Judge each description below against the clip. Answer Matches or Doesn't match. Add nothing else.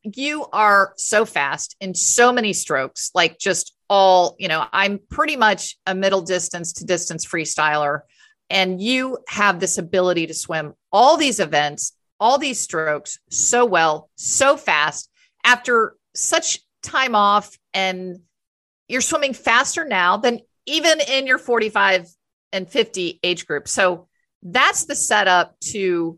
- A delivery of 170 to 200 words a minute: Doesn't match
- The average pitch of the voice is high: Matches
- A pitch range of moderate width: Doesn't match